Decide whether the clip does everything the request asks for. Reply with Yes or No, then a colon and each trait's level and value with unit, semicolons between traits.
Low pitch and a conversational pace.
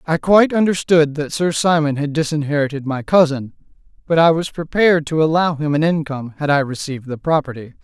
No: medium, 155 Hz; average, 185 wpm